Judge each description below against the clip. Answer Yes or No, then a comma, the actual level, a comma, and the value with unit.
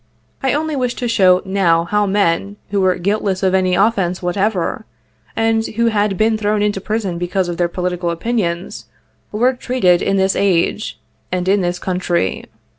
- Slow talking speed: No, average, 170 wpm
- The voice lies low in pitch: No, high, 195 Hz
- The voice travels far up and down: No, average, 3.2 semitones